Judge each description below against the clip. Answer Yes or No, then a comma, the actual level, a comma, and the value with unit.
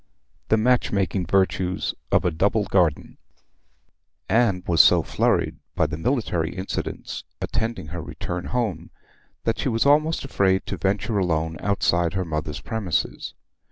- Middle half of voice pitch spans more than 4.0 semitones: Yes, average, 4.8 semitones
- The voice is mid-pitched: No, very low, 95 Hz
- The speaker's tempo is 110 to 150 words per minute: Yes, average, 140 wpm